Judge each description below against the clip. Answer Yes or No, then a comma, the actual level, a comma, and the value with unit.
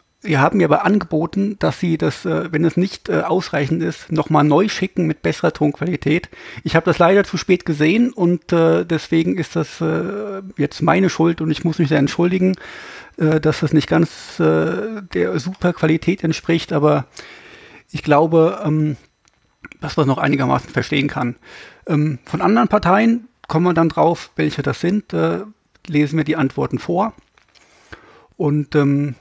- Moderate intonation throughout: Yes, average, 3.6 semitones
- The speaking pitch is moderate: Yes, medium, 165 Hz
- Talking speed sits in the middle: Yes, average, 150 wpm